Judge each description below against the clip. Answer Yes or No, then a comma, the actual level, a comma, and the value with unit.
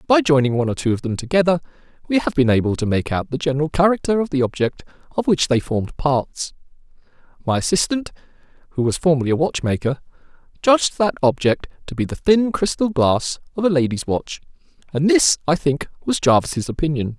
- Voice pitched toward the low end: No, medium, 150 Hz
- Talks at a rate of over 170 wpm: Yes, average, 180 wpm